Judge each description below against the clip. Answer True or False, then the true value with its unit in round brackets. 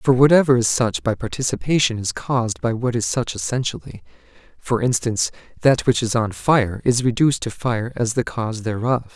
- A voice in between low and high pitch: False (120 Hz)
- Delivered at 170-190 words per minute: True (185 wpm)